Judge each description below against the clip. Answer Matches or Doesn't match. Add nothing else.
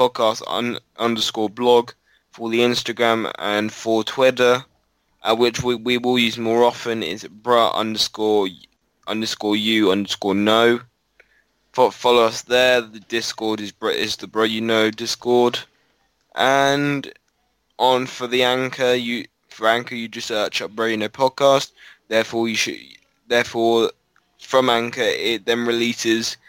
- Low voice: Matches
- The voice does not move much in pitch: Matches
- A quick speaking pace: Doesn't match